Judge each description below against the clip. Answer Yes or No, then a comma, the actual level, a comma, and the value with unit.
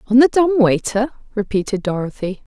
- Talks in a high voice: Yes, high, 225 Hz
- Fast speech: No, average, 140 wpm